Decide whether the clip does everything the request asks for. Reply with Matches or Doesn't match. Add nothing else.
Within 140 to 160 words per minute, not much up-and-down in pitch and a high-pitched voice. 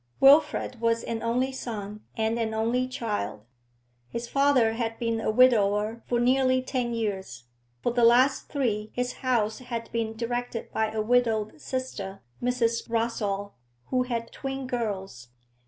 Matches